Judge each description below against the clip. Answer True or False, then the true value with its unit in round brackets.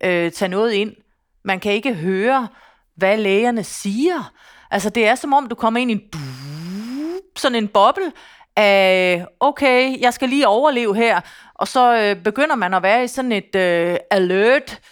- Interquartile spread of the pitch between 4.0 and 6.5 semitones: True (4.9 semitones)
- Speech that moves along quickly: False (170 wpm)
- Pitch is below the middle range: False (215 Hz)